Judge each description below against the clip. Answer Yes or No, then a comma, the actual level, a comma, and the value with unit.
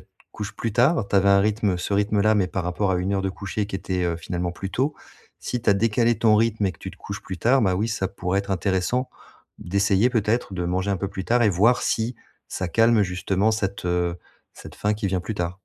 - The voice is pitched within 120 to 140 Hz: No, low, 100 Hz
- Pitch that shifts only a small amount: No, average, 3.0 semitones